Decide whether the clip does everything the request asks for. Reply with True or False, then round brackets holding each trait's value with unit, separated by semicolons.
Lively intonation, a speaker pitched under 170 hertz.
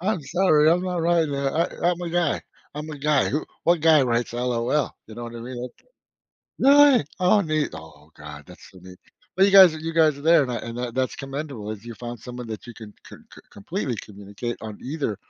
True (5.8 semitones; 135 Hz)